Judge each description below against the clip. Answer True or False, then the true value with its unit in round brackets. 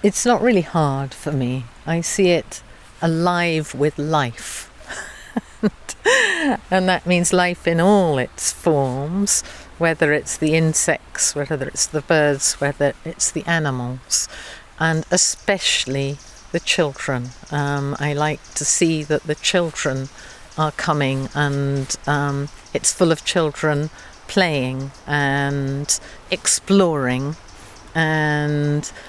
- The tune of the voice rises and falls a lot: False (3.1 semitones)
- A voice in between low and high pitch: True (150 Hz)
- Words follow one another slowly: True (115 wpm)